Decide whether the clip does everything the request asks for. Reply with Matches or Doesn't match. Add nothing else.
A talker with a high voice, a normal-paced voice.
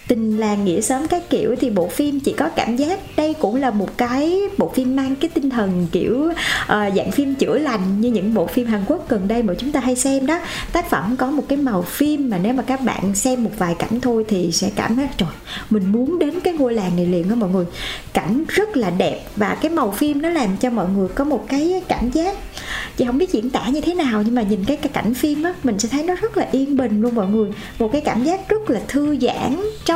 Doesn't match